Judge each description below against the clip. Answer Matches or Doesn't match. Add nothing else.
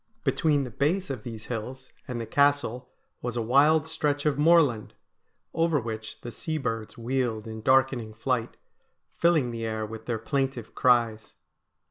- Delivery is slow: Doesn't match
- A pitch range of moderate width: Matches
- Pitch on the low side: Matches